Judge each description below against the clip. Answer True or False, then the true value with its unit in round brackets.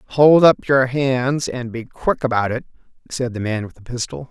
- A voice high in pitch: False (125 Hz)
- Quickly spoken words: True (210 wpm)